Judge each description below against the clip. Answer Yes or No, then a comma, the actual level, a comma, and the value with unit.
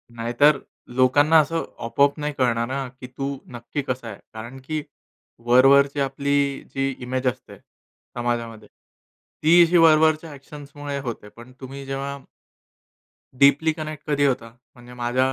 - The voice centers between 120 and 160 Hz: Yes, low, 135 Hz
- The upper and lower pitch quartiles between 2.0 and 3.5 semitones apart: Yes, average, 2.9 semitones